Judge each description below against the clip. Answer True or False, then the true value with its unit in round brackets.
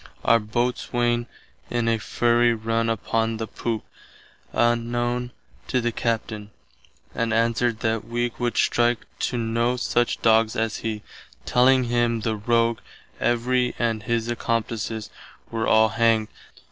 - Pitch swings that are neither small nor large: False (1.1 semitones)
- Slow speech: True (130 wpm)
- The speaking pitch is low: True (115 Hz)